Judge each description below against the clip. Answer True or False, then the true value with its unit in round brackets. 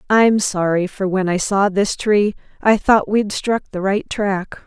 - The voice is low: False (200 Hz)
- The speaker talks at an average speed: True (195 wpm)